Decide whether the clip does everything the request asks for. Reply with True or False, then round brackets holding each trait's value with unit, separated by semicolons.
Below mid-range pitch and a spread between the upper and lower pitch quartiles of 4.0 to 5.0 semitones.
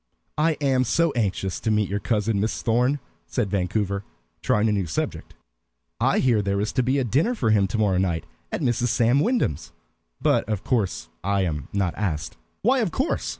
True (110 Hz; 4.6 semitones)